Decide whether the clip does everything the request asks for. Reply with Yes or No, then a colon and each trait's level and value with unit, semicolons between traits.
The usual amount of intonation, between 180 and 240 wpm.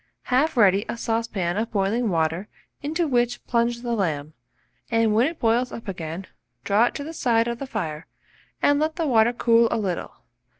Yes: average, 4.0 semitones; average, 185 wpm